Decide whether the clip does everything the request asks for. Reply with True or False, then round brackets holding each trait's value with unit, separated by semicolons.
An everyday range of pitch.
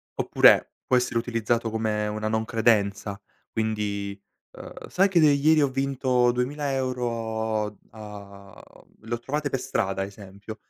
True (3.4 semitones)